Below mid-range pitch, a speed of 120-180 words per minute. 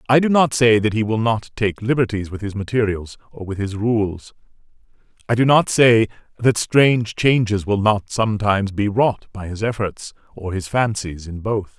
No: low, 110 Hz; average, 190 wpm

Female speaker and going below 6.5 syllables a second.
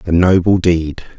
No: male; 4.0 syllables/s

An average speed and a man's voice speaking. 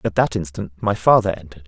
No: fast, 215 wpm; male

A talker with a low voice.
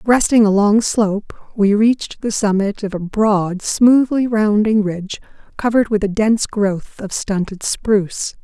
No: high, 210 Hz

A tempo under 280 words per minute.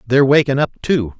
Yes: average, 200 wpm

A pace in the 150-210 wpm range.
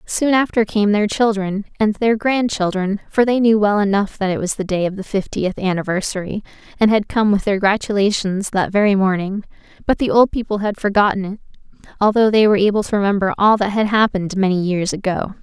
Yes: average, 200 wpm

